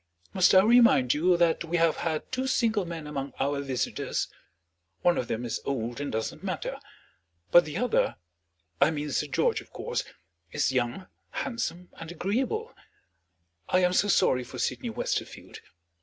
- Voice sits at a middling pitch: Yes, medium, 165 Hz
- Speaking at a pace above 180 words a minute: No, average, 160 wpm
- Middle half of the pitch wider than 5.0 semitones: Yes, wide, 5.5 semitones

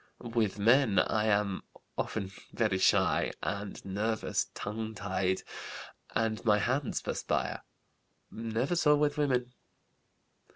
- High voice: No, low, 110 Hz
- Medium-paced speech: No, slow, 110 wpm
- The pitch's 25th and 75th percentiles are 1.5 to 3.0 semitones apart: No, average, 3.5 semitones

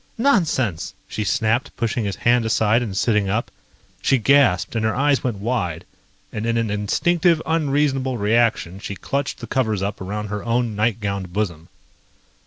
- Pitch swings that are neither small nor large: Yes, average, 4.1 semitones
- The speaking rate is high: No, average, 160 wpm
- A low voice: Yes, low, 115 Hz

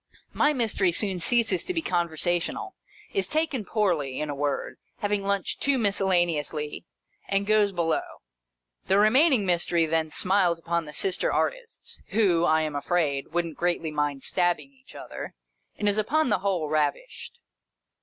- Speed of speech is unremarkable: Yes, average, 155 wpm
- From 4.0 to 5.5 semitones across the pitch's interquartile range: Yes, average, 4.8 semitones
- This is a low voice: No, medium, 180 Hz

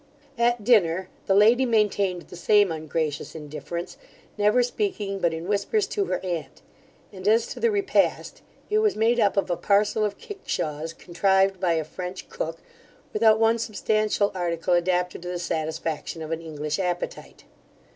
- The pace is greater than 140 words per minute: Yes, average, 160 wpm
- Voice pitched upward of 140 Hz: Yes, high, 190 Hz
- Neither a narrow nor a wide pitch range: Yes, average, 4.5 semitones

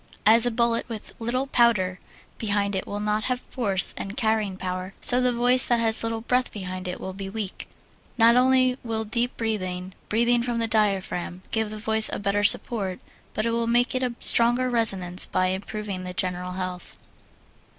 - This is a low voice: No, high, 220 Hz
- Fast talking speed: No, average, 185 wpm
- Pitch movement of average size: Yes, average, 3.8 semitones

